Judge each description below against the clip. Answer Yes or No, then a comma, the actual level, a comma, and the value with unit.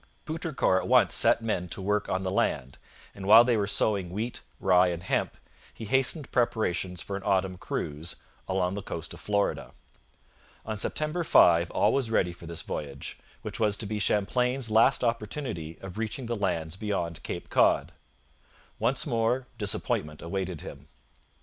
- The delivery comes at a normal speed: Yes, average, 165 wpm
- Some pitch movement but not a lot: Yes, average, 4.4 semitones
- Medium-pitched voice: No, low, 100 Hz